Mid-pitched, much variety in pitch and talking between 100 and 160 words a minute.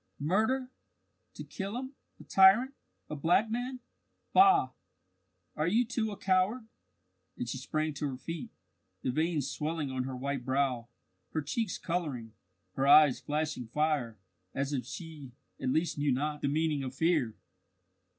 Yes: medium, 155 Hz; wide, 5.8 semitones; average, 150 wpm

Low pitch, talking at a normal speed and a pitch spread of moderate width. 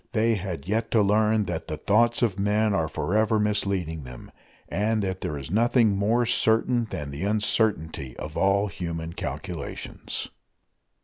Yes: low, 100 Hz; average, 150 wpm; average, 4.7 semitones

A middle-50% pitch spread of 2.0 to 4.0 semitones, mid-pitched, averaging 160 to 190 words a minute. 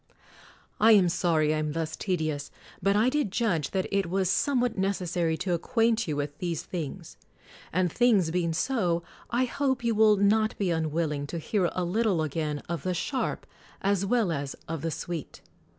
No: average, 5.0 semitones; medium, 180 Hz; average, 185 wpm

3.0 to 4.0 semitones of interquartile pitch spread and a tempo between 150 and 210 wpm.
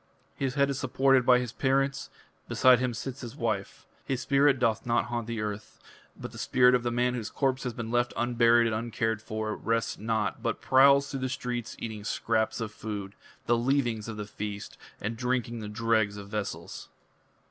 No: narrow, 2.6 semitones; average, 190 wpm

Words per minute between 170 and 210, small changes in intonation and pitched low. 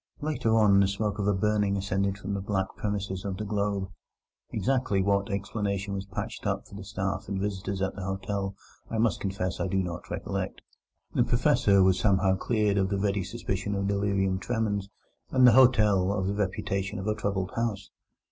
Yes: average, 190 wpm; narrow, 1.4 semitones; low, 100 Hz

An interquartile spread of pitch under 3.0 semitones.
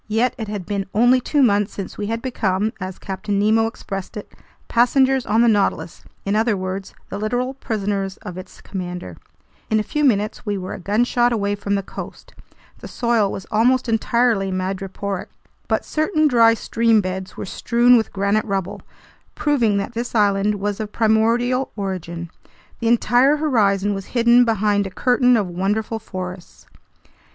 No: average, 3.3 semitones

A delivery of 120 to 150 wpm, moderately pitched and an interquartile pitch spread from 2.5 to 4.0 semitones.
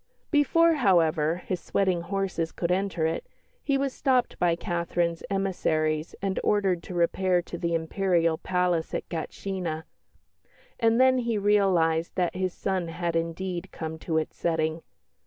Yes: average, 145 wpm; medium, 175 Hz; average, 2.9 semitones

